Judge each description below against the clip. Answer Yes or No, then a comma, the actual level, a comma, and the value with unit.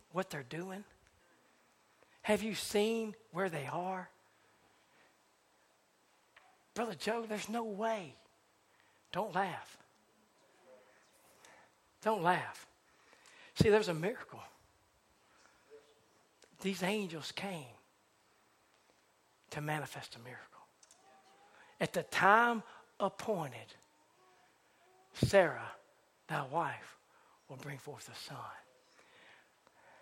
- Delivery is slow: Yes, slow, 80 wpm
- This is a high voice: Yes, high, 195 Hz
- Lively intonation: Yes, wide, 6.1 semitones